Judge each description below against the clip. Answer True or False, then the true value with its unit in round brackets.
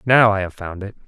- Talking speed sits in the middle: False (280 wpm)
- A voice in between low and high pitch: False (100 Hz)